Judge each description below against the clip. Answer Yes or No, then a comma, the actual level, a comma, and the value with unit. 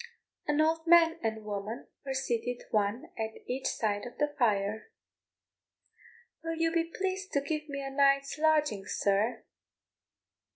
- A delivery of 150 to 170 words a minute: No, average, 140 wpm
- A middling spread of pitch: No, wide, 6.2 semitones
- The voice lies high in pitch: Yes, very high, 275 Hz